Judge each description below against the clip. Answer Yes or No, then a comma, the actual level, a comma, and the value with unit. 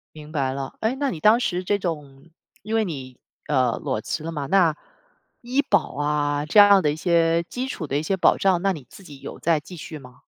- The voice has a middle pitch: Yes, medium, 165 Hz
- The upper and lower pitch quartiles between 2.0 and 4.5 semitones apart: No, average, 5.1 semitones